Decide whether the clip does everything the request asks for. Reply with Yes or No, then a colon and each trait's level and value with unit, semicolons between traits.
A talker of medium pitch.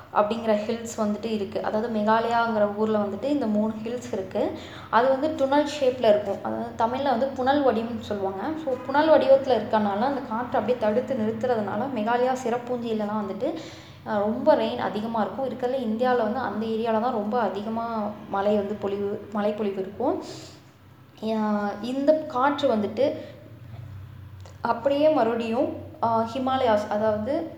No: high, 225 Hz